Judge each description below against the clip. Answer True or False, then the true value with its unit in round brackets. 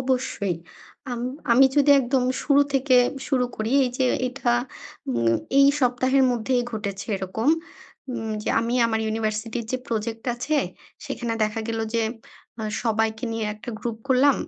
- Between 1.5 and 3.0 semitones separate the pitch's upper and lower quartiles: True (2.7 semitones)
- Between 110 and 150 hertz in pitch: False (235 Hz)